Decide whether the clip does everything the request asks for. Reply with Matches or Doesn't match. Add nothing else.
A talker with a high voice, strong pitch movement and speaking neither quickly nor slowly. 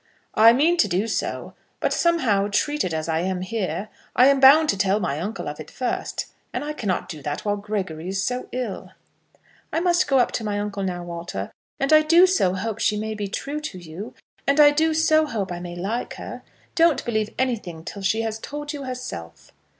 Doesn't match